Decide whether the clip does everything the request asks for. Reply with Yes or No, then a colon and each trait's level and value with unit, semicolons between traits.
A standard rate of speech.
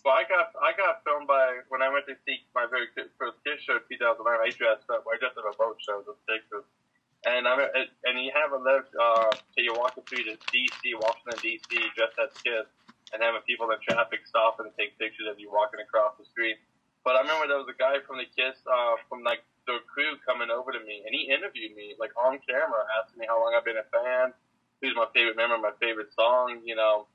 No: fast, 245 wpm